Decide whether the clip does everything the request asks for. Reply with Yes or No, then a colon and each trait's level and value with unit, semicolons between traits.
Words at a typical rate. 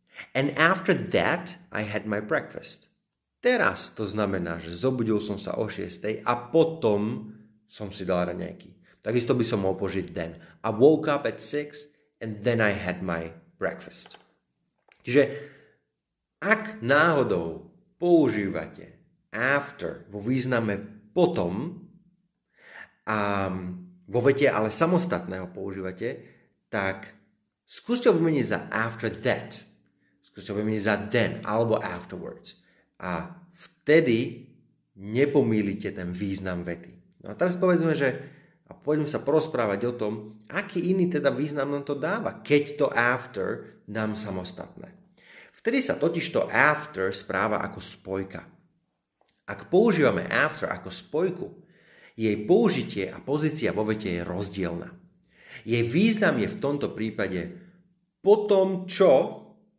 Yes: average, 125 wpm